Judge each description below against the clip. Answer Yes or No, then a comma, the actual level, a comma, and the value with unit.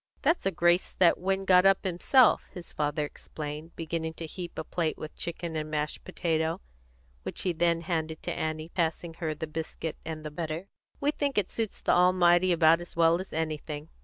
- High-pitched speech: No, medium, 165 Hz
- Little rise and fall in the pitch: Yes, narrow, 2.2 semitones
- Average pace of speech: Yes, average, 190 wpm